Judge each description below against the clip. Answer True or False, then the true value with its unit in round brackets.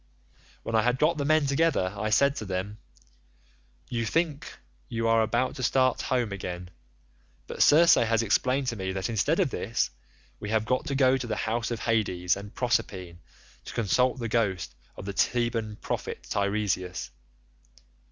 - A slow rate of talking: False (170 wpm)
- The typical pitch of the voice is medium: False (115 Hz)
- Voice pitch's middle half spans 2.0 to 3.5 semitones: False (4.2 semitones)